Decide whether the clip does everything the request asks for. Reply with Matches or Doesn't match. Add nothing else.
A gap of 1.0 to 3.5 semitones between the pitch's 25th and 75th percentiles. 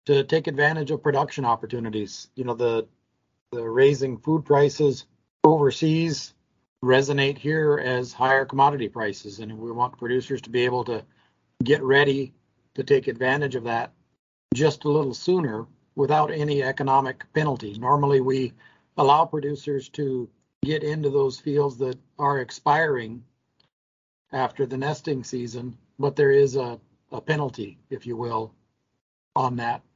Matches